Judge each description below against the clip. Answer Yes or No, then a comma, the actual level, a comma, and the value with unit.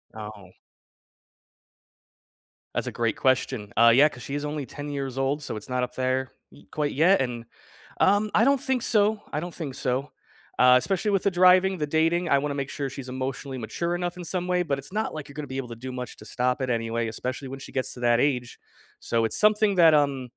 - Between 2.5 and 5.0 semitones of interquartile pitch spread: No, wide, 5.4 semitones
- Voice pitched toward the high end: No, medium, 140 Hz